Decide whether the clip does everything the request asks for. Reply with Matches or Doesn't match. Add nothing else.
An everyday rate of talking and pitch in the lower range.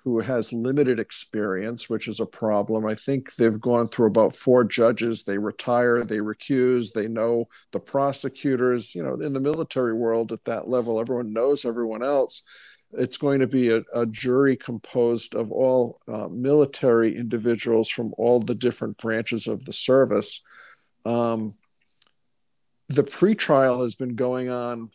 Matches